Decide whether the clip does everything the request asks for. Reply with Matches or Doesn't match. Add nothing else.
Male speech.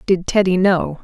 Doesn't match